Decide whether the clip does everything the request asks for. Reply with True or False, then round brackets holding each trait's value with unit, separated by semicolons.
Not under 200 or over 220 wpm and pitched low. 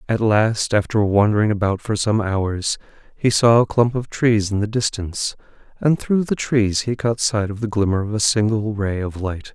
True (205 wpm; 110 Hz)